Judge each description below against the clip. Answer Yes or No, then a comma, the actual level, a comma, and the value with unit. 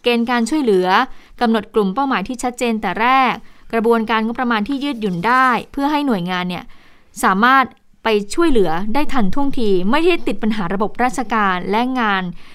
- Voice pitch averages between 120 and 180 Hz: No, high, 235 Hz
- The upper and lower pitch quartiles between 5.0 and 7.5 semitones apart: No, average, 3.8 semitones